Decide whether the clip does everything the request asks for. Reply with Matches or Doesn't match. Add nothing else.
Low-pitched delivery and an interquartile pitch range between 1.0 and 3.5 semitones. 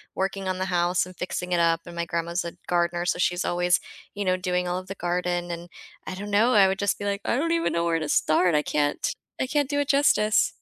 Doesn't match